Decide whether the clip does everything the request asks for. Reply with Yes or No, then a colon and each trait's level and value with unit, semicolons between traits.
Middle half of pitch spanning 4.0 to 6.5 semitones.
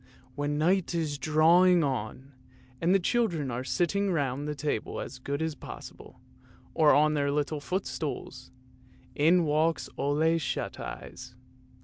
No: average, 3.0 semitones